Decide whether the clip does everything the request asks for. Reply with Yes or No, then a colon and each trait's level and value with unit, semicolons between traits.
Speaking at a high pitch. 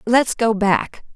Yes: high, 225 Hz